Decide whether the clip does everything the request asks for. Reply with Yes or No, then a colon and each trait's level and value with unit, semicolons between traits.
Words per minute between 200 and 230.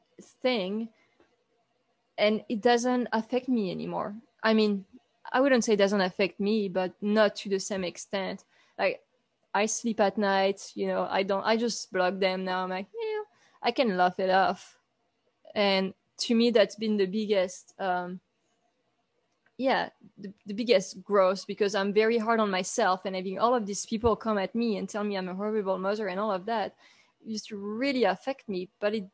No: average, 185 wpm